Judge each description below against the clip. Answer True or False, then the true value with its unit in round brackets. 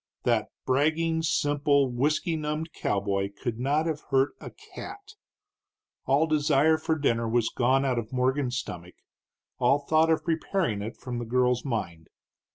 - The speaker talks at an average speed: True (150 wpm)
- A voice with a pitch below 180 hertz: True (135 Hz)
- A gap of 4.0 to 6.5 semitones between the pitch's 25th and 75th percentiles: True (4.4 semitones)